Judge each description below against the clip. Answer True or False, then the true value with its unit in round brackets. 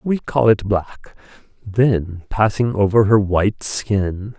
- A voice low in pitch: True (105 Hz)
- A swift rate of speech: False (135 wpm)